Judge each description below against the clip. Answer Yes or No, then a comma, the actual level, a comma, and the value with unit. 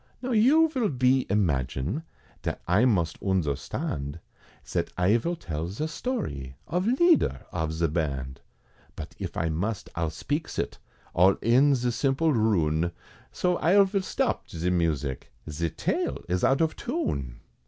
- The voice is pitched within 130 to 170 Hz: No, low, 100 Hz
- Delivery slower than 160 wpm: Yes, average, 150 wpm